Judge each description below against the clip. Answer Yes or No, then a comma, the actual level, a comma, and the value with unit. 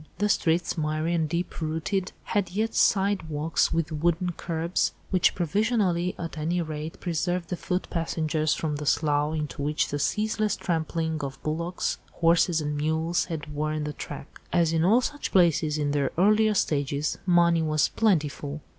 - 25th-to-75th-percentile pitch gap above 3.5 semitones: No, average, 2.7 semitones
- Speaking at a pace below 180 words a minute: Yes, average, 165 wpm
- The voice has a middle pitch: Yes, medium, 165 Hz